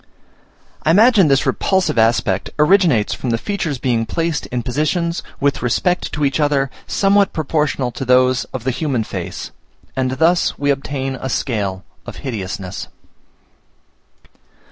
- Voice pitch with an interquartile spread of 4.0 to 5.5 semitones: Yes, average, 4.9 semitones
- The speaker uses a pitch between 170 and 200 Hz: No, low, 135 Hz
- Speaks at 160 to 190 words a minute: No, average, 140 wpm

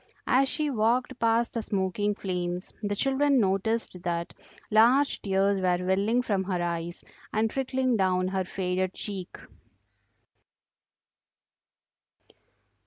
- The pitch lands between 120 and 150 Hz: No, high, 200 Hz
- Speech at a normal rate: No, slow, 110 wpm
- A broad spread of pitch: No, average, 4.1 semitones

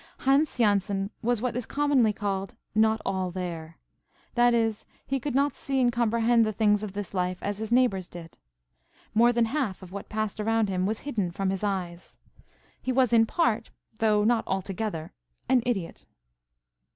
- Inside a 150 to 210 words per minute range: Yes, average, 175 wpm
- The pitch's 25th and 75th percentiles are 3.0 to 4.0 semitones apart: Yes, average, 3.7 semitones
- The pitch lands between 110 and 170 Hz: No, high, 215 Hz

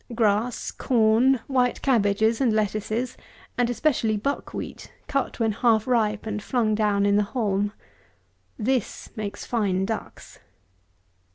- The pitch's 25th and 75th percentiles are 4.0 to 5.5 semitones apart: No, average, 2.9 semitones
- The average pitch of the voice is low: No, high, 220 Hz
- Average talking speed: No, slow, 125 wpm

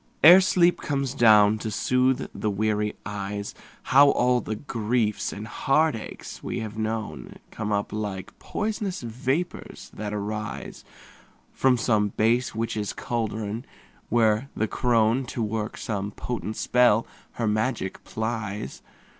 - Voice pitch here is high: No, low, 110 Hz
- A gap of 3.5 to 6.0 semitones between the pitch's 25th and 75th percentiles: No, average, 2.8 semitones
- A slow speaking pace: Yes, slow, 130 wpm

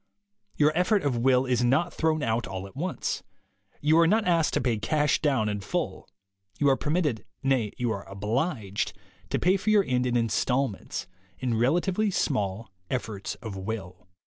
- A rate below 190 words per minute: Yes, average, 180 wpm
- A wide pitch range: Yes, wide, 6.3 semitones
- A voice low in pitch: Yes, low, 125 Hz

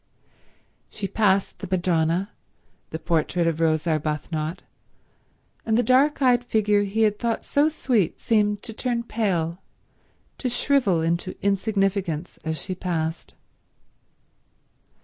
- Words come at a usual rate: No, slow, 120 wpm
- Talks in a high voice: Yes, high, 195 Hz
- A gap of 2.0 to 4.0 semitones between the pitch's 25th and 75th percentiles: No, average, 5.1 semitones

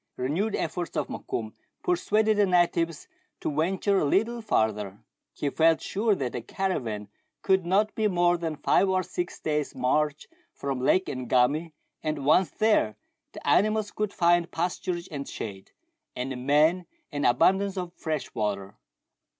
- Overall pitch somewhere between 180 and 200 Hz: No, medium, 165 Hz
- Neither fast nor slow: Yes, average, 150 wpm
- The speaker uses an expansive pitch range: Yes, wide, 5.8 semitones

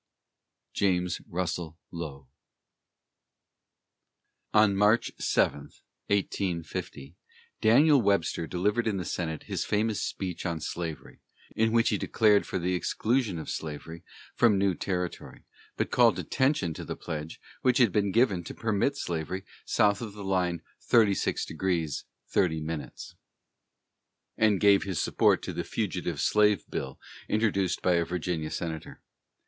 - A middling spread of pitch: Yes, average, 4.0 semitones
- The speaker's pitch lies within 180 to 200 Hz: No, very low, 95 Hz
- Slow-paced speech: Yes, slow, 130 wpm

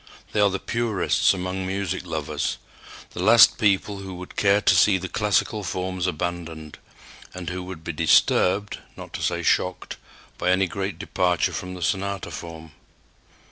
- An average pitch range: No, narrow, 2.1 semitones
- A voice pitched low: Yes, very low, 95 Hz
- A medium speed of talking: Yes, average, 160 wpm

